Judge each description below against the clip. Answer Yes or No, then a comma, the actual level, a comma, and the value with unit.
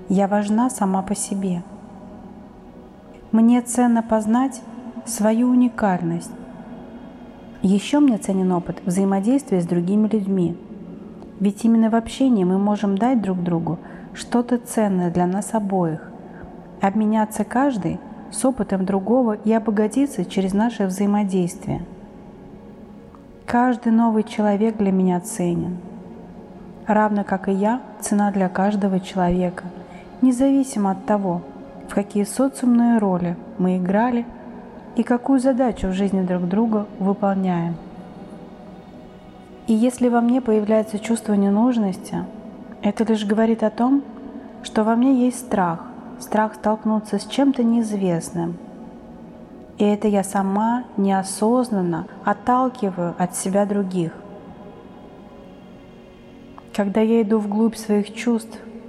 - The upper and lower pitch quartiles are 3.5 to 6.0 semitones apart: No, average, 3.0 semitones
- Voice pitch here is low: No, high, 210 Hz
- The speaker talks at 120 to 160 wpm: No, slow, 110 wpm